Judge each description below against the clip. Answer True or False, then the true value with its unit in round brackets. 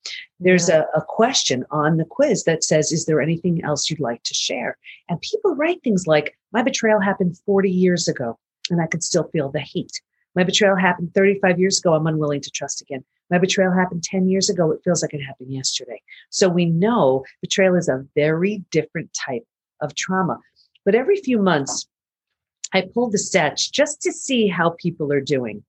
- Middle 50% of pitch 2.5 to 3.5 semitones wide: False (4.4 semitones)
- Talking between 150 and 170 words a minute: False (195 wpm)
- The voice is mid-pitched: True (175 Hz)